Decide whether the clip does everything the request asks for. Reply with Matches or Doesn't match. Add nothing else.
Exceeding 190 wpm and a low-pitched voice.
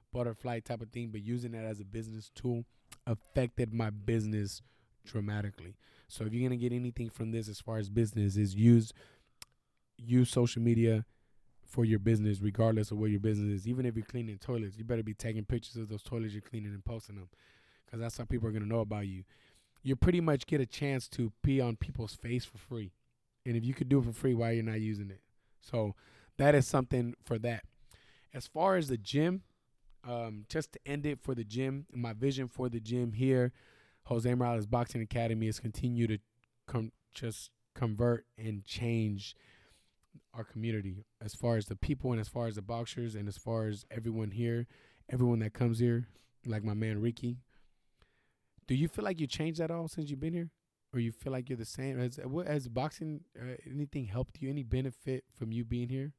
Matches